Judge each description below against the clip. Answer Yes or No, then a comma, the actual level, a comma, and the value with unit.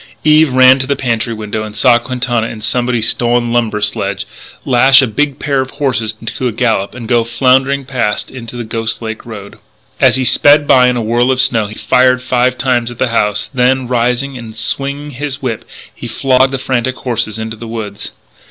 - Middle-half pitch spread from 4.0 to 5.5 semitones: No, narrow, 2.5 semitones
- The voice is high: No, low, 125 Hz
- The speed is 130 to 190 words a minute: No, average, 200 wpm